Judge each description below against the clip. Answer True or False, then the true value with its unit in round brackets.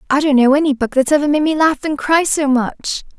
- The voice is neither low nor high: False (285 Hz)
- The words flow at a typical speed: False (265 wpm)